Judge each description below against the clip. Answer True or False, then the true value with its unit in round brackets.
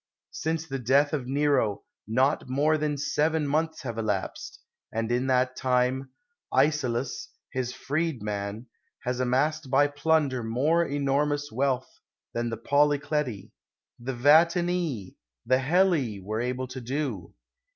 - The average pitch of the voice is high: False (135 Hz)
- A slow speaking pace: True (130 wpm)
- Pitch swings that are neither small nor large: True (3.3 semitones)